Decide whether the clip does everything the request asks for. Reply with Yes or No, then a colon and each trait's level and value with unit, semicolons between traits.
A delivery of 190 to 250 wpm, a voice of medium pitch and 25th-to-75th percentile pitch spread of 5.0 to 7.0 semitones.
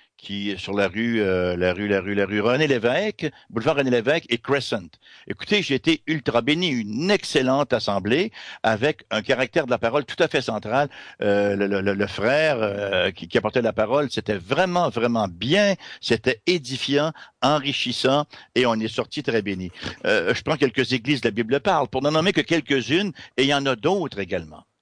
No: average, 195 wpm; low, 130 Hz; wide, 5.6 semitones